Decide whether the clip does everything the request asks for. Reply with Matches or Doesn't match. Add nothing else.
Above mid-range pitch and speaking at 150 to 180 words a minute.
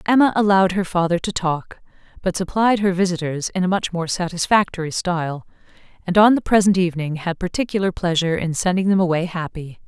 Doesn't match